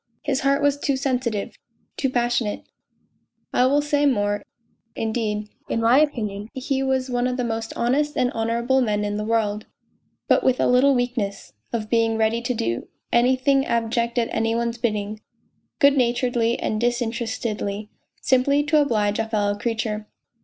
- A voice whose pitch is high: Yes, high, 235 Hz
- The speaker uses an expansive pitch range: No, average, 3.0 semitones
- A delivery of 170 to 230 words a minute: No, average, 160 wpm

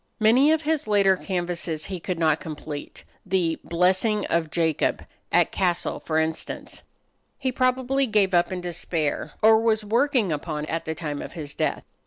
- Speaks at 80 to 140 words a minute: No, average, 165 wpm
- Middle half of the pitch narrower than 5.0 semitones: No, average, 5.3 semitones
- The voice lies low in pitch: No, medium, 180 Hz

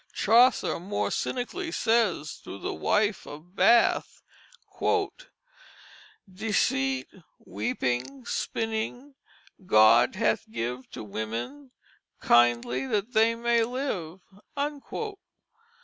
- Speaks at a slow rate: Yes, slow, 85 wpm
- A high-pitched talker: Yes, high, 220 Hz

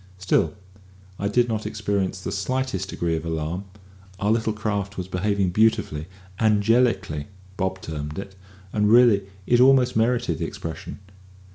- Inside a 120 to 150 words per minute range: Yes, average, 140 wpm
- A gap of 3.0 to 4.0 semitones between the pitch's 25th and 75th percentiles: Yes, average, 3.7 semitones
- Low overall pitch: Yes, low, 100 Hz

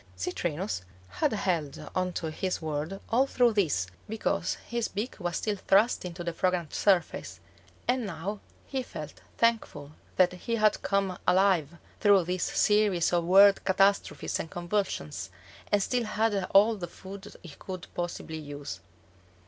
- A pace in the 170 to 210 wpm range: No, average, 150 wpm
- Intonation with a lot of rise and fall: No, average, 3.6 semitones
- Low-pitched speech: No, high, 190 Hz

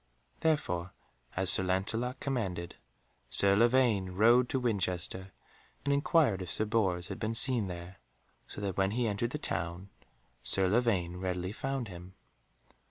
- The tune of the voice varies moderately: Yes, average, 4.6 semitones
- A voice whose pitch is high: No, low, 100 Hz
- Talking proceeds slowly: No, average, 145 wpm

